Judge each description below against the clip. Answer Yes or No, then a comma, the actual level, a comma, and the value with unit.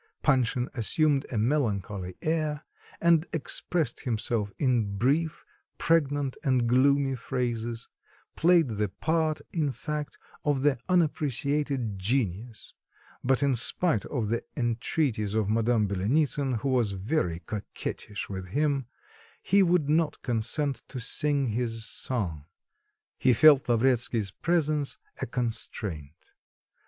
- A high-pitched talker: No, low, 130 Hz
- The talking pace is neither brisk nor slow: No, slow, 115 wpm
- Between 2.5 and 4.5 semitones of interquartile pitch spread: No, average, 5.1 semitones